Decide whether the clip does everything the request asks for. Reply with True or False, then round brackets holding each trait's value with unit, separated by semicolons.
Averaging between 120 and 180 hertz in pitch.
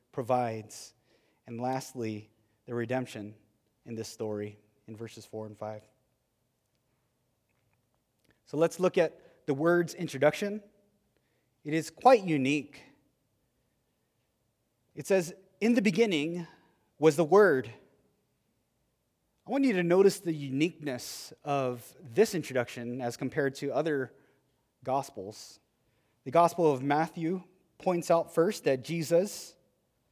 True (135 Hz)